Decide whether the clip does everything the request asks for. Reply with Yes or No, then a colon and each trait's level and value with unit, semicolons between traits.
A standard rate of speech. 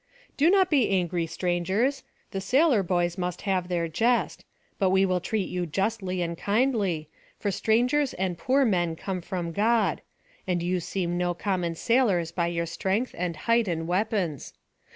Yes: average, 165 wpm